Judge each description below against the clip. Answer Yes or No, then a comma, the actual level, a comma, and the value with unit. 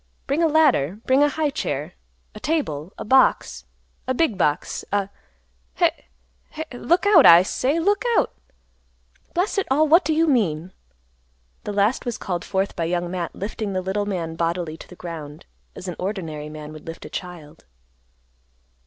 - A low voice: No, high, 190 Hz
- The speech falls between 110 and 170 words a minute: Yes, average, 160 wpm